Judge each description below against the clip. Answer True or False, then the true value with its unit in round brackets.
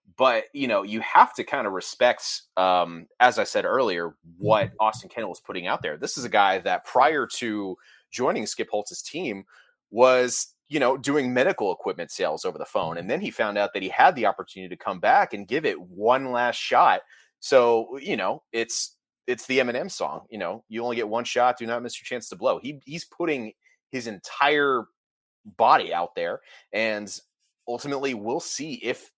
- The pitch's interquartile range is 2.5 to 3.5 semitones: False (4.0 semitones)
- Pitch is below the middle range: True (120 Hz)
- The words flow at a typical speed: True (195 wpm)